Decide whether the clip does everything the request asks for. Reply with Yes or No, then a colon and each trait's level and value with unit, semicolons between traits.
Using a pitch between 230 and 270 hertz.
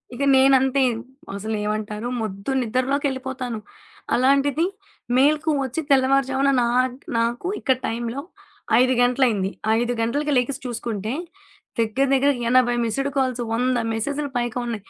Yes: very high, 255 Hz